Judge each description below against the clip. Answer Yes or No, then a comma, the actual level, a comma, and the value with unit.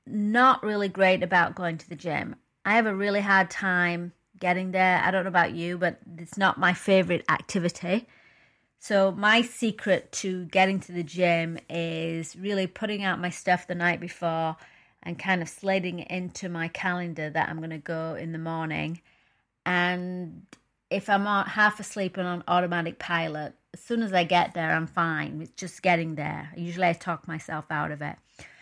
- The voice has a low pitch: No, medium, 180 Hz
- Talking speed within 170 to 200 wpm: Yes, average, 185 wpm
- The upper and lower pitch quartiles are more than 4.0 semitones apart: No, narrow, 2.4 semitones